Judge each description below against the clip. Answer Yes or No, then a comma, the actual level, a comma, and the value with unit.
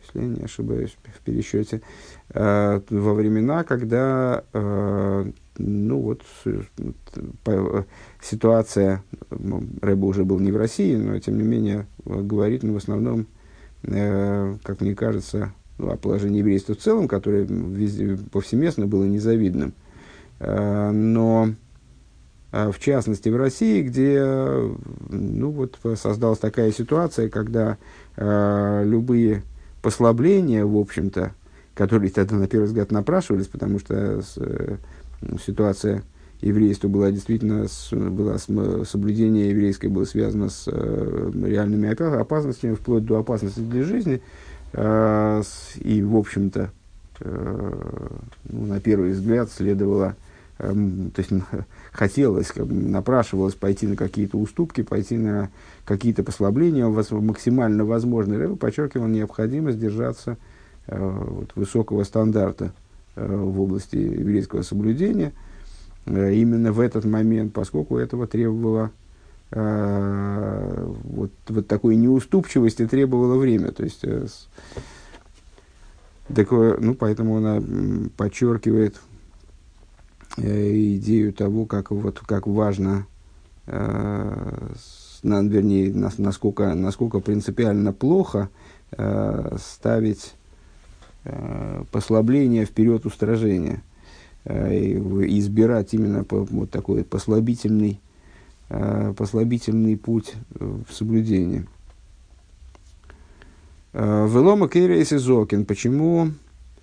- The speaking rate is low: Yes, slow, 95 wpm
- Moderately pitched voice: No, low, 105 Hz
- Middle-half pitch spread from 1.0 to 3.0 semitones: Yes, narrow, 2.4 semitones